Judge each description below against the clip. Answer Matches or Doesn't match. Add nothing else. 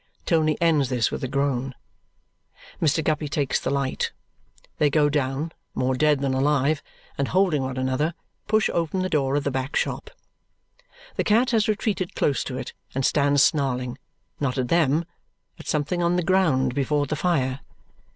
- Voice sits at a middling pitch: Matches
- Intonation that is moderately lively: Matches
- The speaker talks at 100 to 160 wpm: Doesn't match